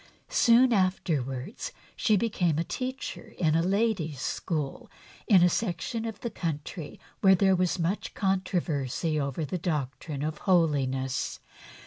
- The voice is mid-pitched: Yes, medium, 175 Hz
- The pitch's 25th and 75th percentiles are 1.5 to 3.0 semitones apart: No, average, 4.8 semitones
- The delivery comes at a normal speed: No, slow, 130 wpm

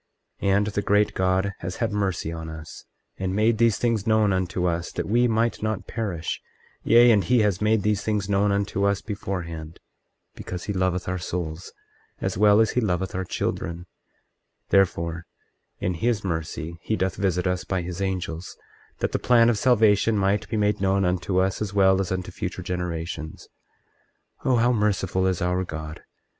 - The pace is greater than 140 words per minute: Yes, average, 180 wpm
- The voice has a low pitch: Yes, very low, 95 Hz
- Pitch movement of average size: Yes, average, 3.0 semitones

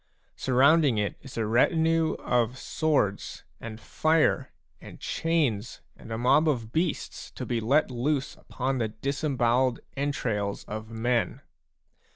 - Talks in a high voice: No, low, 125 Hz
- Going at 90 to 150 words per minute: Yes, average, 140 wpm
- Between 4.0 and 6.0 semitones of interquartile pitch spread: Yes, average, 4.8 semitones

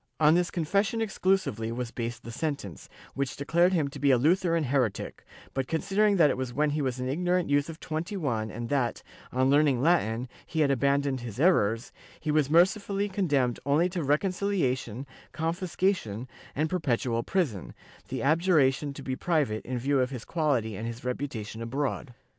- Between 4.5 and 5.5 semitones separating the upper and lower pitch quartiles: Yes, average, 5.2 semitones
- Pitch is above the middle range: No, medium, 140 Hz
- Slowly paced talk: No, average, 175 wpm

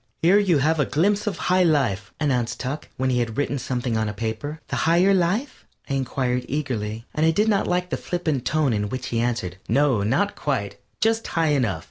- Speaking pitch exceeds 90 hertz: Yes, medium, 140 Hz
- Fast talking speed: Yes, fast, 210 wpm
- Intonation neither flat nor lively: No, wide, 6.2 semitones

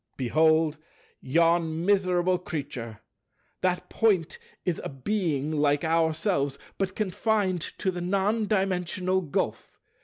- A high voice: No, medium, 175 Hz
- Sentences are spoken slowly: Yes, slow, 110 wpm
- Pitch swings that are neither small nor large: Yes, average, 3.4 semitones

